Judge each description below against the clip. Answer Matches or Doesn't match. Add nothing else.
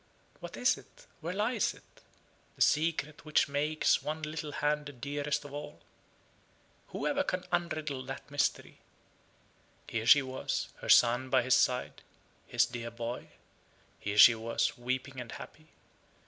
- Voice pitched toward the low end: Doesn't match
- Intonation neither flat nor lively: Matches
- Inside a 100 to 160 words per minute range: Matches